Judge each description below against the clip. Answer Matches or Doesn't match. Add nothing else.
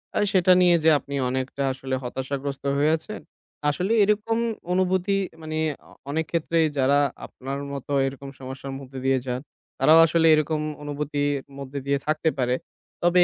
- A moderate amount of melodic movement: Matches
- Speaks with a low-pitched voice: Doesn't match